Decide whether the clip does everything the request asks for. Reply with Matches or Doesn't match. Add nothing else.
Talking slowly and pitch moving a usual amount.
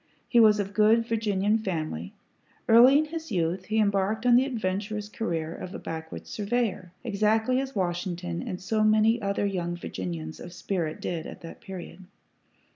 Doesn't match